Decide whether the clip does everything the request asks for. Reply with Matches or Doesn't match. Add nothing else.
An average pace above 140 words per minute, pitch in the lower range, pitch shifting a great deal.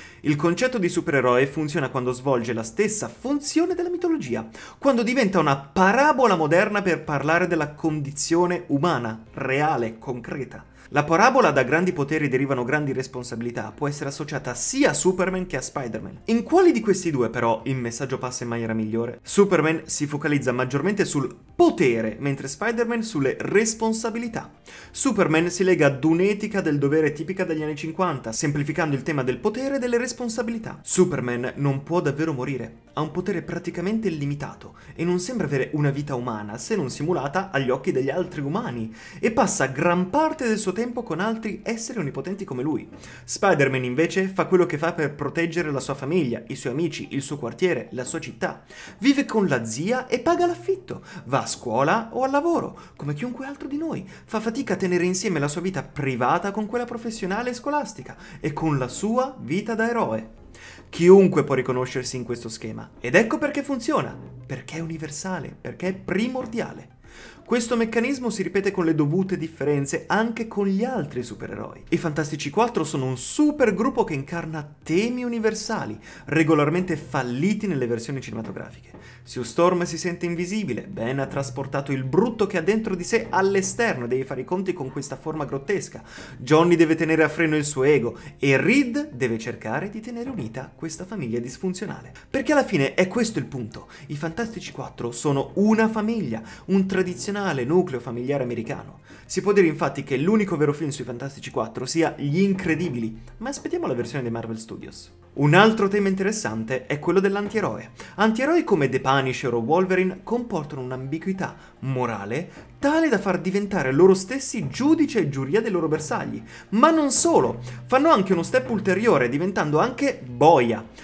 Doesn't match